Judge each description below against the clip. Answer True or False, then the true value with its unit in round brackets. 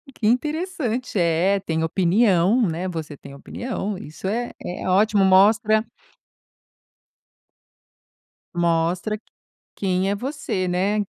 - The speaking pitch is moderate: False (195 Hz)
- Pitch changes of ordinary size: True (3.9 semitones)